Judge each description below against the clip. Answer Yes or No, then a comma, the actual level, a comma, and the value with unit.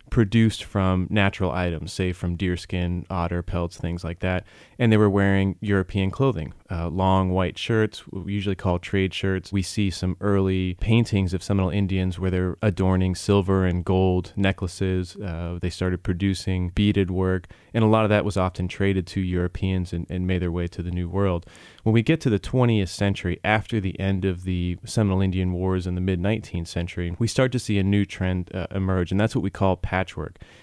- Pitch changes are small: Yes, narrow, 1.9 semitones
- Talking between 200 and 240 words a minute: Yes, fast, 205 wpm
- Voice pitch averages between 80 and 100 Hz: Yes, very low, 95 Hz